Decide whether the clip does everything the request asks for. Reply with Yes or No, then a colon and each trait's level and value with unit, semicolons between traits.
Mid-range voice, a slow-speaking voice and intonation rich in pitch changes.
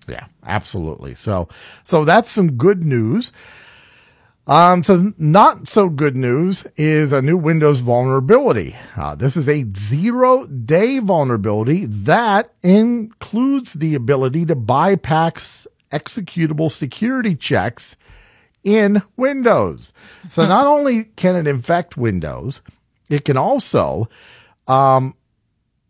Yes: medium, 160 Hz; slow, 110 wpm; wide, 7.6 semitones